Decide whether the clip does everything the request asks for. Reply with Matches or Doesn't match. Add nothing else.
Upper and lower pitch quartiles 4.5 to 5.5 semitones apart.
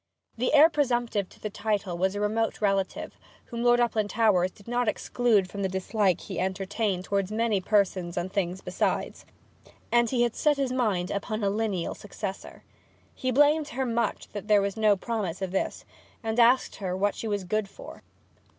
Doesn't match